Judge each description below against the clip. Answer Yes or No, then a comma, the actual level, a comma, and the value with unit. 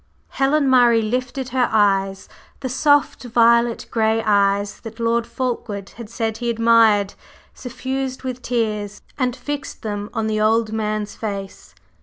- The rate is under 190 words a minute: Yes, average, 140 wpm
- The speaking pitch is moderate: No, high, 230 Hz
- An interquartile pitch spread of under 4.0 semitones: Yes, average, 2.8 semitones